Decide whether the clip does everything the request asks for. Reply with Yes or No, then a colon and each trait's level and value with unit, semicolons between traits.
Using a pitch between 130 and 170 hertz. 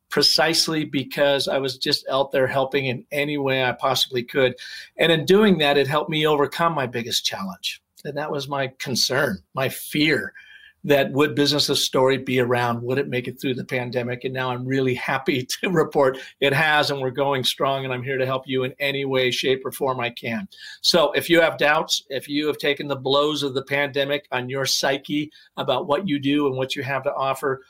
Yes: medium, 140 Hz